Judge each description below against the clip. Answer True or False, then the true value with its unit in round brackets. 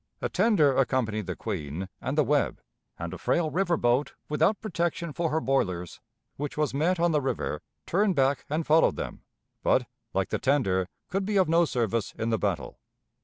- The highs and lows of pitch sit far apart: True (6.8 semitones)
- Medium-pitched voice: True (145 Hz)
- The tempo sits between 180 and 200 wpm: True (185 wpm)